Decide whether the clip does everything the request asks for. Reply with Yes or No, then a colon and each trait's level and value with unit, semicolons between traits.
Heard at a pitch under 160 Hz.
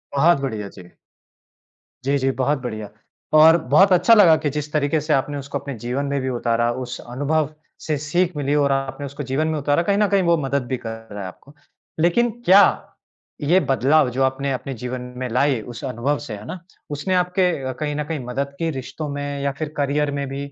Yes: medium, 140 Hz